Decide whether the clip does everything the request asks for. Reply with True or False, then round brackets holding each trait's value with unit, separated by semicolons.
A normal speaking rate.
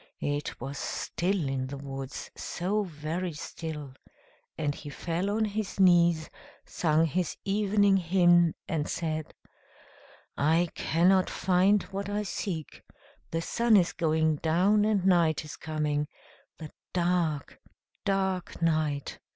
False (125 wpm)